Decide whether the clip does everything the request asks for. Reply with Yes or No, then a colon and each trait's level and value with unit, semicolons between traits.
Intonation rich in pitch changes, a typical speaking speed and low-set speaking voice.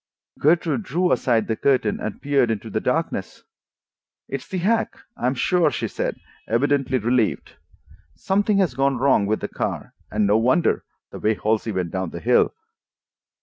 Yes: wide, 6.1 semitones; average, 160 wpm; low, 125 Hz